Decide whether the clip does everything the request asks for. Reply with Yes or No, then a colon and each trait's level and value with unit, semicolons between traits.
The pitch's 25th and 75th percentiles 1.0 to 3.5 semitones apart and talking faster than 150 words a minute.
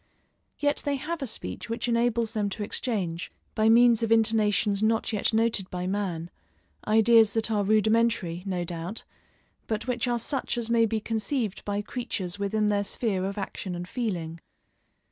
Yes: average, 2.9 semitones; average, 165 wpm